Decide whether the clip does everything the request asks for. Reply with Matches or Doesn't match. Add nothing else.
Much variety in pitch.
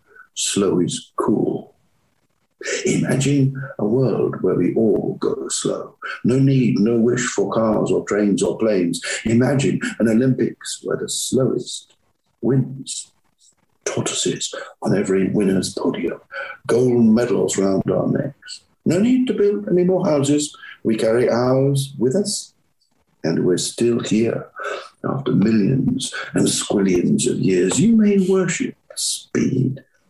Matches